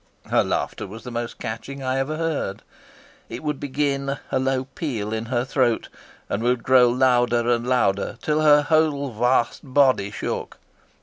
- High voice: No, low, 130 Hz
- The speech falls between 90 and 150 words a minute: No, average, 165 wpm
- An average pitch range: Yes, average, 3.0 semitones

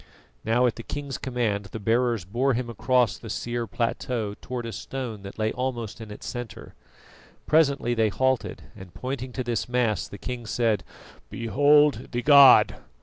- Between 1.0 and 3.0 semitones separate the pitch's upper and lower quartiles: Yes, narrow, 2.5 semitones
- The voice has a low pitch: Yes, low, 120 Hz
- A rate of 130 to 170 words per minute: Yes, average, 165 wpm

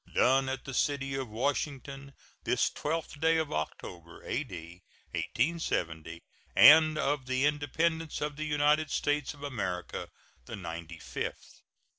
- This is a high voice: No, medium, 140 Hz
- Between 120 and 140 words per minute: Yes, slow, 135 wpm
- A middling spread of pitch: No, wide, 7.0 semitones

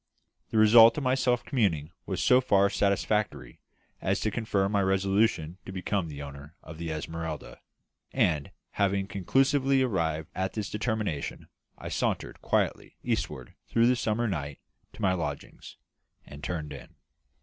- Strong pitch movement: Yes, wide, 5.7 semitones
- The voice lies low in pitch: Yes, very low, 95 Hz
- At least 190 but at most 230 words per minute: No, average, 150 wpm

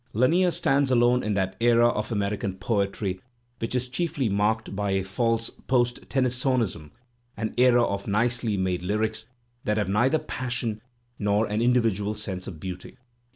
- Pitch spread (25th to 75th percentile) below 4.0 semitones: Yes, average, 3.5 semitones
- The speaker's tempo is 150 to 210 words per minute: Yes, average, 155 wpm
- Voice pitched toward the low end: Yes, low, 110 Hz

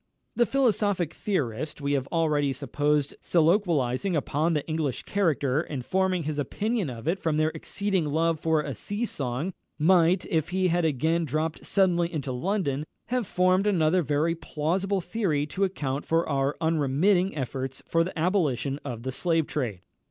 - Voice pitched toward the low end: No, medium, 160 Hz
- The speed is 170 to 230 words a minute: No, average, 160 wpm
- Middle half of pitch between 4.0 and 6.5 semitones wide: Yes, average, 4.3 semitones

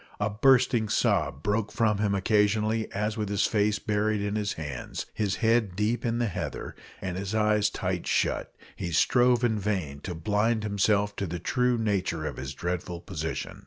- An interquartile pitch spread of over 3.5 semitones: No, average, 2.8 semitones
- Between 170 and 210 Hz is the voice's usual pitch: No, low, 105 Hz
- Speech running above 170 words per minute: Yes, average, 180 wpm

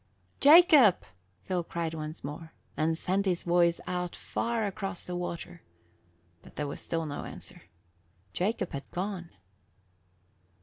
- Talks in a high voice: No, medium, 175 Hz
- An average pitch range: Yes, average, 3.1 semitones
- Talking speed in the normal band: No, slow, 130 wpm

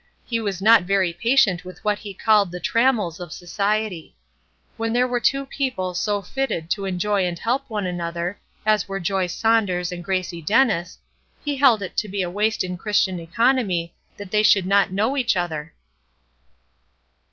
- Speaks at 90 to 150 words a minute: No, average, 175 wpm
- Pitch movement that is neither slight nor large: Yes, average, 4.0 semitones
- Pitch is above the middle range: Yes, high, 200 Hz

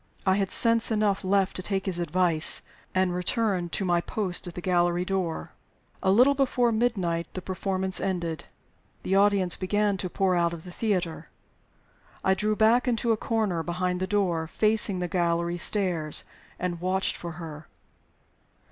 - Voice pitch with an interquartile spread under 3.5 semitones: Yes, average, 2.9 semitones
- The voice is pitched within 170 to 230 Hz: Yes, medium, 185 Hz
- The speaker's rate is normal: Yes, average, 165 wpm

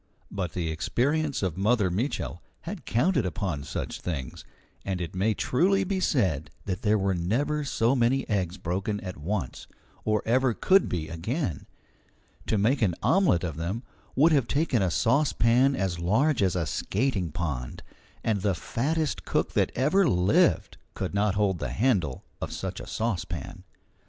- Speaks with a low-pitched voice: Yes, low, 105 Hz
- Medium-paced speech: Yes, average, 160 wpm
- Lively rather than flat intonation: Yes, wide, 6.9 semitones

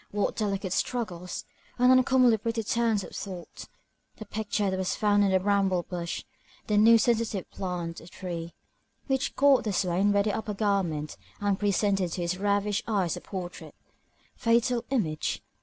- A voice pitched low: No, high, 200 Hz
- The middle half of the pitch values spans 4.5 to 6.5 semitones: No, average, 3.3 semitones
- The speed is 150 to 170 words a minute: Yes, average, 160 wpm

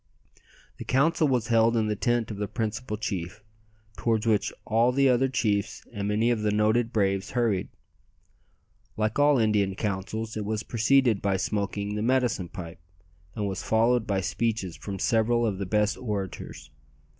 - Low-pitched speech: Yes, low, 110 Hz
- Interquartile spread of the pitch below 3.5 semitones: Yes, average, 2.8 semitones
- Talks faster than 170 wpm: No, average, 165 wpm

